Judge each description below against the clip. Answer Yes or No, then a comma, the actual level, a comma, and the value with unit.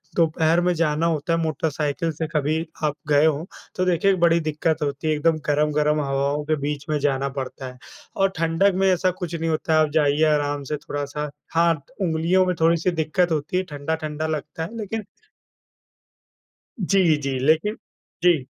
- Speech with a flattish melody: Yes, narrow, 2.2 semitones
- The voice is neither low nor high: Yes, medium, 155 Hz